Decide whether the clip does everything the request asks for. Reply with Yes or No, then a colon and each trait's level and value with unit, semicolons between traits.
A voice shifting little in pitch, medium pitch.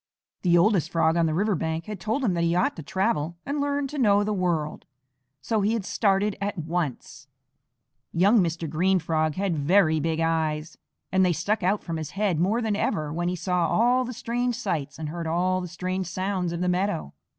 No: average, 3.8 semitones; medium, 180 Hz